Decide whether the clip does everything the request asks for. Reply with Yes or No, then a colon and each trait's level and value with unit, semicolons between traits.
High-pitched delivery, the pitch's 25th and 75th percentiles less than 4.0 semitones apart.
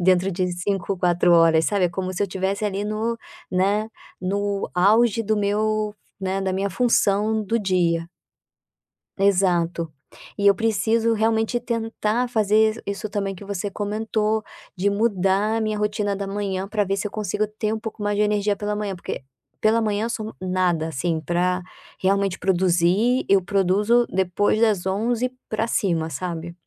Yes: high, 200 Hz; narrow, 2.6 semitones